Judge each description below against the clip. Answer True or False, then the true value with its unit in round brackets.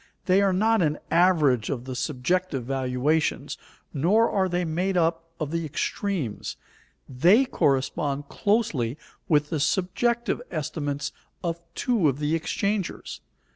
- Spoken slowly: True (130 wpm)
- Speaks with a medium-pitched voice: True (165 Hz)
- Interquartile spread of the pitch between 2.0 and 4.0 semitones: False (4.9 semitones)